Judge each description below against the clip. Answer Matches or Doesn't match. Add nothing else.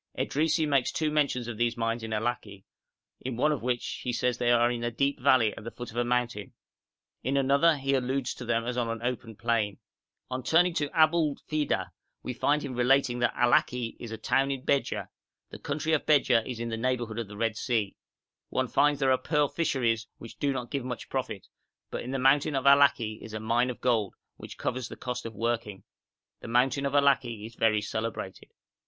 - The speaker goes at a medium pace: Doesn't match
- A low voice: Matches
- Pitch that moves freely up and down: Doesn't match